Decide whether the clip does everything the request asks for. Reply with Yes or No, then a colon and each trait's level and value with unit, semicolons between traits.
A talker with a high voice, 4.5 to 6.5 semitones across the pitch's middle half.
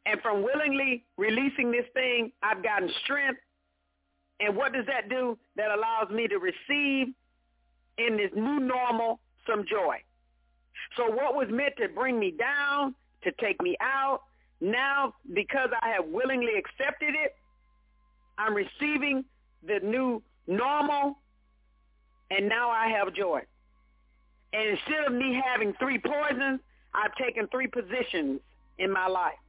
Yes: high, 240 Hz; average, 5.2 semitones